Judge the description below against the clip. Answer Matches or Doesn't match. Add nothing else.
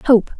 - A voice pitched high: Matches